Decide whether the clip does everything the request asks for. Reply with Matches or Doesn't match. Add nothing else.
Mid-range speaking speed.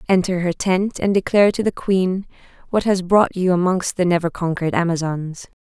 Matches